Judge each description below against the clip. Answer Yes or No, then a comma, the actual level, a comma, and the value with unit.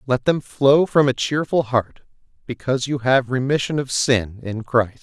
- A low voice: Yes, low, 130 Hz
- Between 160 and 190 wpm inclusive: Yes, average, 180 wpm